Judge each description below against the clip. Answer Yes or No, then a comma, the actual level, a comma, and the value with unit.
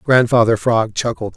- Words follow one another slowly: Yes, slow, 130 wpm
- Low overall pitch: Yes, low, 115 Hz